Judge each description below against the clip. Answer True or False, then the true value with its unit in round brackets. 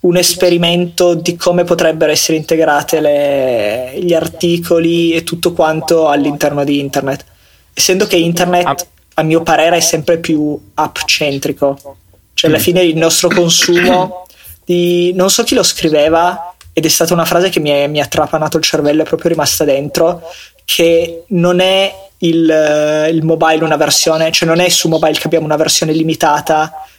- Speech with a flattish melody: True (2.3 semitones)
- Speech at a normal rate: True (160 wpm)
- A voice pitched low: False (165 Hz)